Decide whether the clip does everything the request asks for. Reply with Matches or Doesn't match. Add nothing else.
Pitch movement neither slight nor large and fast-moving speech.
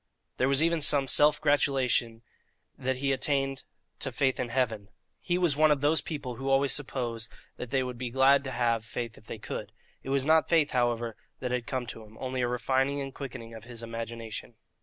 Matches